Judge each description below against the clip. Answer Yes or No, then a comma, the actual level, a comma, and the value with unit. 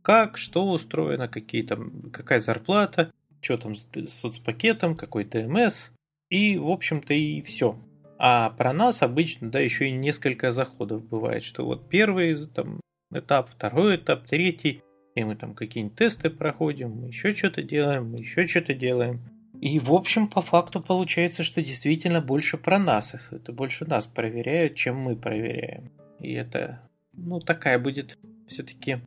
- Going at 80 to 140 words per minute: No, average, 155 wpm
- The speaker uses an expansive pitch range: Yes, wide, 6.1 semitones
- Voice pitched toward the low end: No, medium, 150 Hz